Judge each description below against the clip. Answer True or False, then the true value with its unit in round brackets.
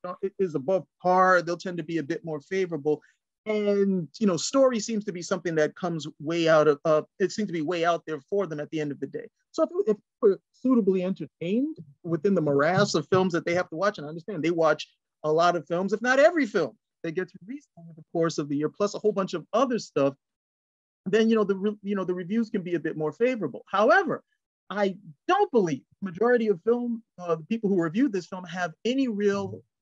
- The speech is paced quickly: True (235 wpm)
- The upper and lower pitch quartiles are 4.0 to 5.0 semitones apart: True (4.7 semitones)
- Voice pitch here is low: False (185 Hz)